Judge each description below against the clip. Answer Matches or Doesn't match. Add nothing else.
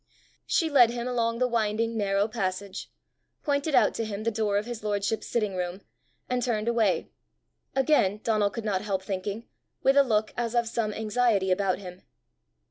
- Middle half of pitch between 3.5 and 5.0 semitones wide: Doesn't match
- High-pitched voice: Matches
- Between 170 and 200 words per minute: Matches